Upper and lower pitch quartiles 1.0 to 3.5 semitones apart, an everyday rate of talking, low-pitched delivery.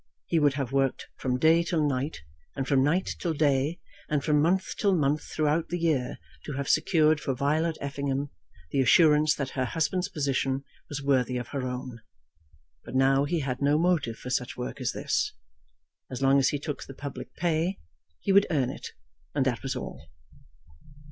No: average, 3.0 semitones; average, 185 wpm; medium, 145 Hz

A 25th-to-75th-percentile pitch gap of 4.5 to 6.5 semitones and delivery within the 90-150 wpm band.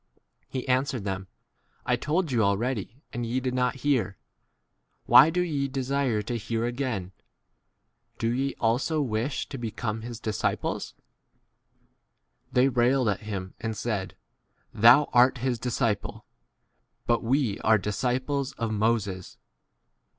No: average, 3.5 semitones; average, 145 wpm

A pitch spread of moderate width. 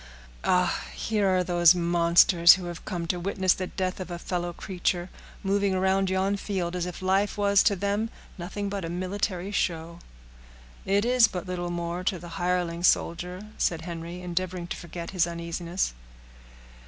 No: narrow, 1.9 semitones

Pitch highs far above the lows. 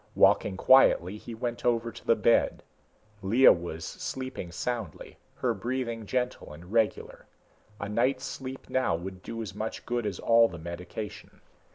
No: average, 4.5 semitones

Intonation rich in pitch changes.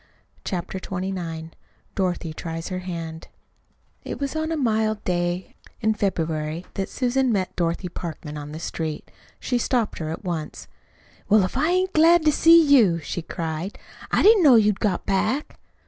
Yes: wide, 6.9 semitones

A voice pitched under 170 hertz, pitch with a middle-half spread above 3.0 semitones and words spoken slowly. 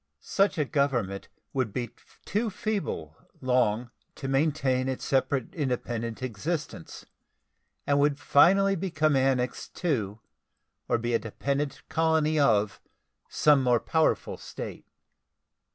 Yes: low, 135 Hz; average, 4.3 semitones; slow, 115 wpm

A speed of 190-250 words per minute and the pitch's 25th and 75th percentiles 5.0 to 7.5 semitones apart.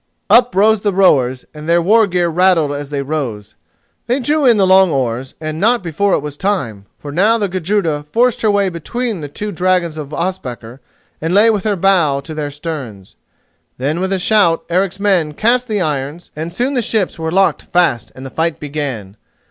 Yes: average, 200 wpm; wide, 5.6 semitones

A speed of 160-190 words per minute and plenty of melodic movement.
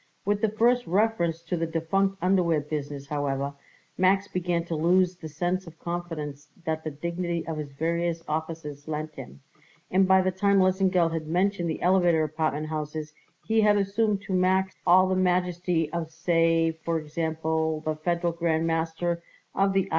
No: average, 170 wpm; average, 2.8 semitones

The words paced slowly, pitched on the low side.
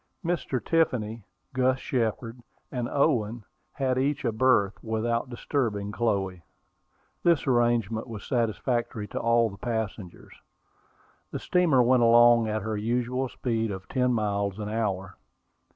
Yes: slow, 130 wpm; low, 115 Hz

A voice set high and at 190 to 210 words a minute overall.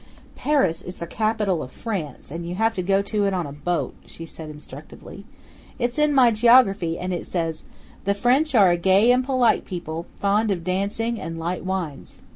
Yes: high, 195 Hz; average, 195 wpm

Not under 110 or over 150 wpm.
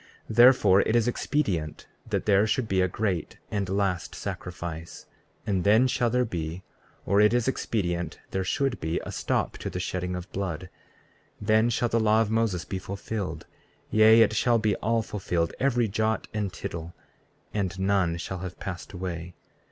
No: average, 175 wpm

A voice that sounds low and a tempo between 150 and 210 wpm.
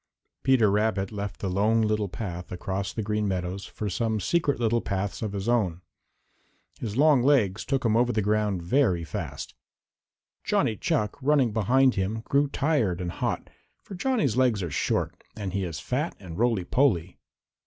Yes: low, 105 Hz; average, 170 wpm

